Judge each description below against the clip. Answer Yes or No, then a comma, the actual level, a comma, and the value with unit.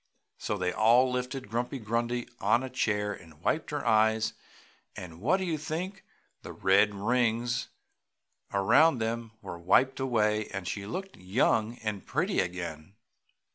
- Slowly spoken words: No, average, 145 wpm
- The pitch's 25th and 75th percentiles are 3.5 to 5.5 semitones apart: Yes, average, 4.2 semitones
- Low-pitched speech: Yes, low, 110 Hz